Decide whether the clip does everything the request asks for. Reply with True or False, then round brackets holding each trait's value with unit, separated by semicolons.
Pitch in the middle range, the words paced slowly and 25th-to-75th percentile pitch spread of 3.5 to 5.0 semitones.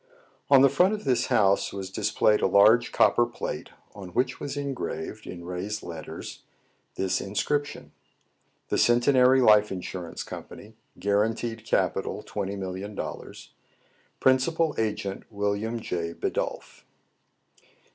False (105 Hz; 115 wpm; 4.6 semitones)